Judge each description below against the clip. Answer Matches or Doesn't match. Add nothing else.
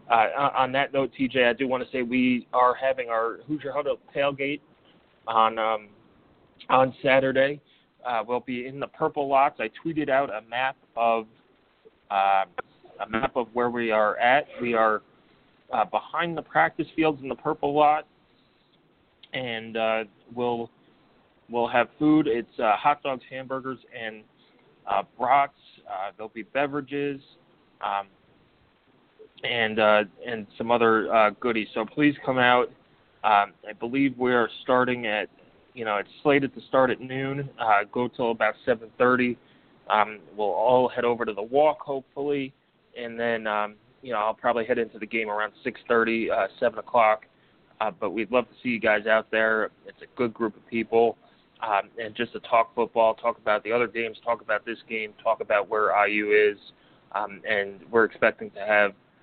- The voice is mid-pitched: Doesn't match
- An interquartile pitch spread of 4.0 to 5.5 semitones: Doesn't match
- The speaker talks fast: Doesn't match